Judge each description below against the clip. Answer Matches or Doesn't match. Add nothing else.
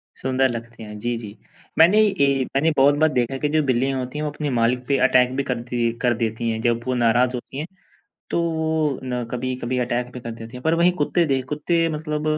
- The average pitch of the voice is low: Matches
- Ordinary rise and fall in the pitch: Matches